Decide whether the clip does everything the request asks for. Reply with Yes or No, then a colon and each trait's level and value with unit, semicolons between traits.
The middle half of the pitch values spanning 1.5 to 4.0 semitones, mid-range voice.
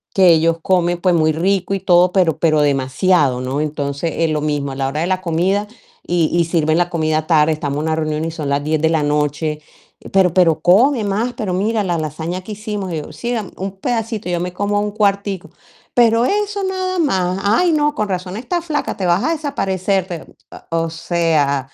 No: average, 4.4 semitones; medium, 175 Hz